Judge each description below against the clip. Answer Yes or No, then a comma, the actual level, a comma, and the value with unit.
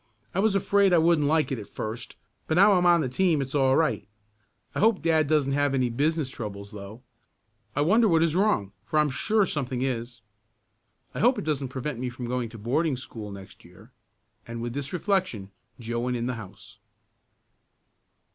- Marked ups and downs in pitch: Yes, wide, 5.7 semitones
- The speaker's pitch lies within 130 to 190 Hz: Yes, low, 135 Hz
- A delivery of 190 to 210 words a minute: Yes, average, 195 wpm